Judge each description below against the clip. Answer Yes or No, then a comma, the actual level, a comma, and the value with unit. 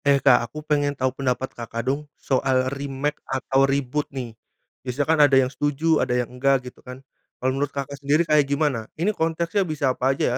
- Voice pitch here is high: No, low, 135 Hz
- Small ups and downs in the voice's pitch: Yes, narrow, 2.1 semitones